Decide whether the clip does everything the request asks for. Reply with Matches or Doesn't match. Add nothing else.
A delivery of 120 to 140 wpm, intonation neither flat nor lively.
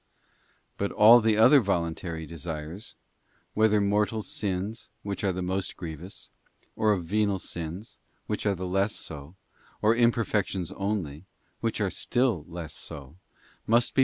Matches